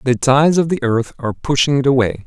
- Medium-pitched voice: No, low, 130 Hz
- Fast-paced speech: Yes, fast, 240 wpm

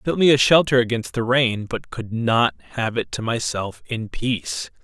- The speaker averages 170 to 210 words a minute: Yes, average, 200 wpm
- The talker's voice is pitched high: No, low, 115 Hz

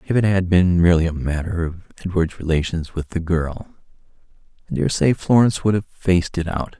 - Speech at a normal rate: Yes, average, 195 wpm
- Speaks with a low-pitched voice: Yes, very low, 90 Hz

